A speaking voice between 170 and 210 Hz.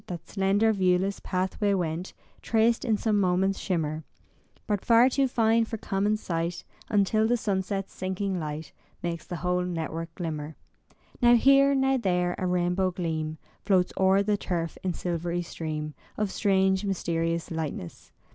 Yes: medium, 185 Hz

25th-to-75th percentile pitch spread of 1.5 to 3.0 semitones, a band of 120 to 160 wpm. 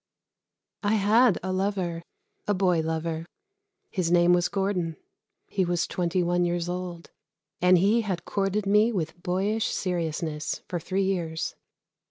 Yes: narrow, 2.4 semitones; average, 140 wpm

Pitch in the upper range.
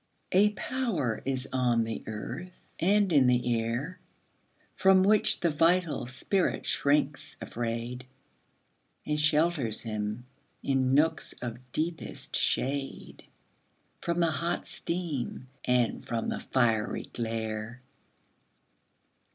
No: low, 135 Hz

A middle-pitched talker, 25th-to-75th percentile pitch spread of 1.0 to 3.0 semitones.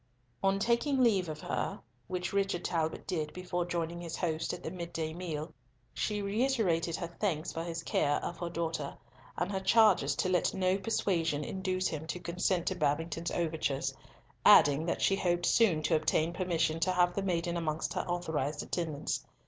Yes: medium, 175 Hz; narrow, 2.5 semitones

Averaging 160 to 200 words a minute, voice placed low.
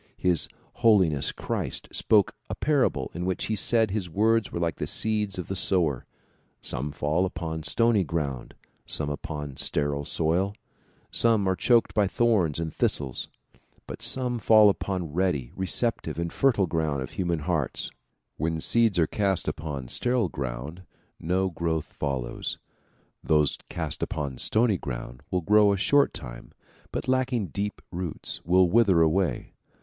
No: average, 150 wpm; very low, 90 Hz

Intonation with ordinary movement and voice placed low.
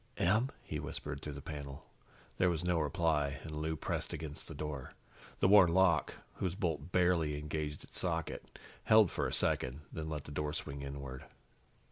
Yes: average, 3.1 semitones; very low, 75 Hz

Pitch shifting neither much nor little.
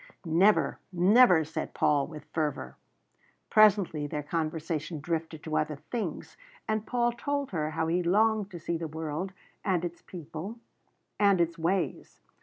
Yes: average, 4.1 semitones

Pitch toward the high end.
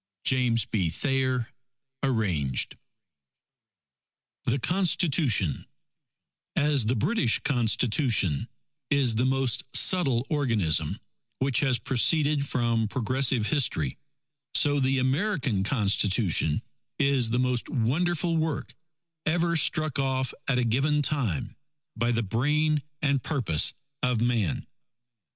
No: low, 130 Hz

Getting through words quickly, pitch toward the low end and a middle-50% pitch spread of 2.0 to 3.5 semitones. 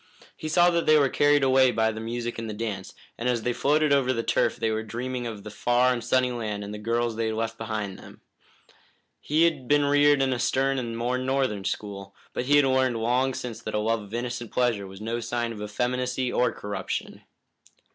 Yes: fast, 225 wpm; low, 120 Hz; average, 2.8 semitones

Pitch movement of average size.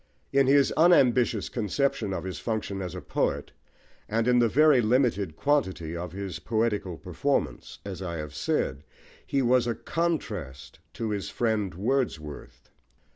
No: wide, 5.7 semitones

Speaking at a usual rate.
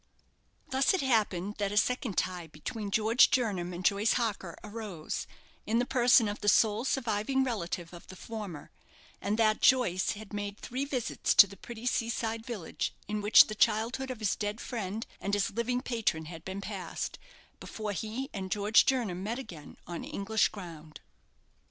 Yes: average, 175 wpm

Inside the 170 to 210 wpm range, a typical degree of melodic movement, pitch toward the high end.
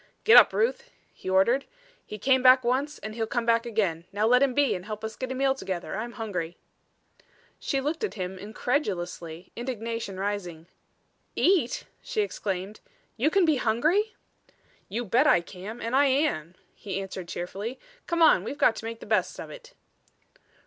No: average, 180 wpm; wide, 5.8 semitones; high, 230 Hz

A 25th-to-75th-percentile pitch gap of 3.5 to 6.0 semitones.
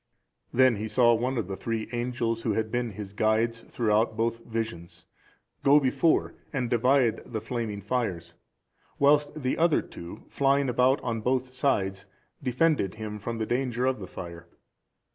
No: average, 3.1 semitones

